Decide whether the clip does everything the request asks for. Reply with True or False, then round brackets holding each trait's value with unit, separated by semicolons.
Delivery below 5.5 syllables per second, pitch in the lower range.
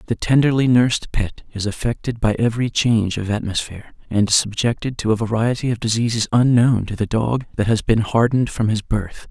False (5.6 syllables/s; 115 Hz)